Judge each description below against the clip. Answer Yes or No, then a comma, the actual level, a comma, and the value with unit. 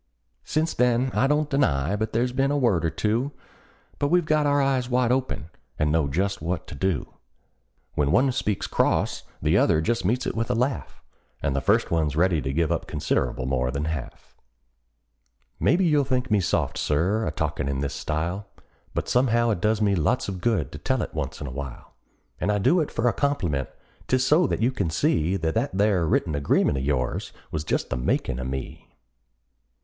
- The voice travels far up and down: Yes, wide, 8.7 semitones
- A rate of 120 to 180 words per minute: No, fast, 205 wpm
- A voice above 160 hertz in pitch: No, low, 100 Hz